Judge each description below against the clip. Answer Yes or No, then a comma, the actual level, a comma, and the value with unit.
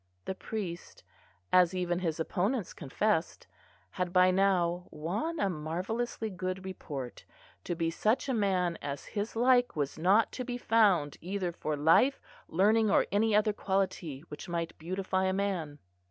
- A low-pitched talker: No, medium, 185 Hz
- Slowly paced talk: No, average, 155 wpm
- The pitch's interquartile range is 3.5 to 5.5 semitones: Yes, average, 3.9 semitones